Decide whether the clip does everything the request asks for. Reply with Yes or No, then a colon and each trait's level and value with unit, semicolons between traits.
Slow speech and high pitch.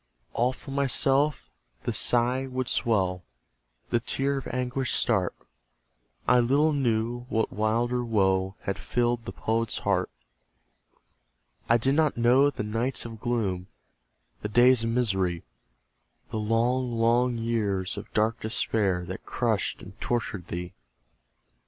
No: slow, 130 wpm; low, 115 Hz